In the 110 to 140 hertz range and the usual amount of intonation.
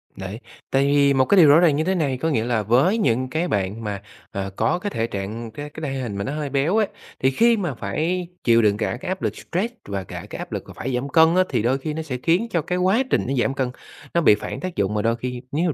No: low, 135 Hz; wide, 6.7 semitones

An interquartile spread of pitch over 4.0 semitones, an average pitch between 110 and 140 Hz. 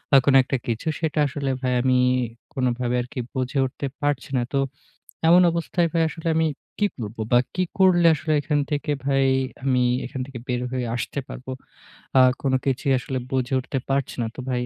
No: average, 2.8 semitones; low, 135 Hz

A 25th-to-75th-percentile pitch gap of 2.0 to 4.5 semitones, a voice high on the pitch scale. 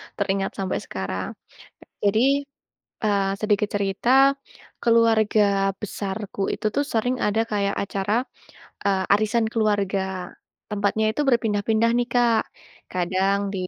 Yes: narrow, 2.6 semitones; high, 210 Hz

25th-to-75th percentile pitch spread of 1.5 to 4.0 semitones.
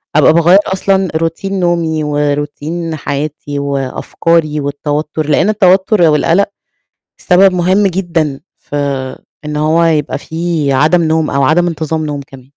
Yes: average, 2.9 semitones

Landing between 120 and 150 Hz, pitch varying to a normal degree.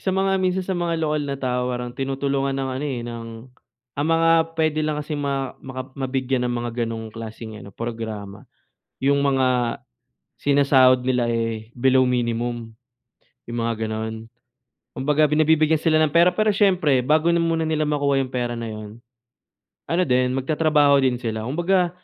Yes: low, 135 Hz; average, 4.5 semitones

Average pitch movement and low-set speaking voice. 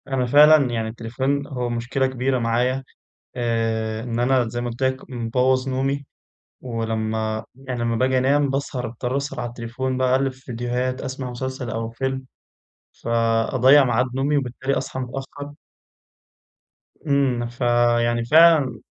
No: narrow, 2.1 semitones; low, 125 Hz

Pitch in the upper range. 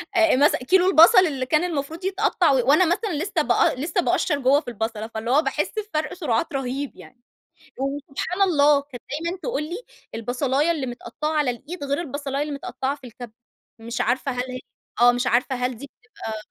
Yes: very high, 280 Hz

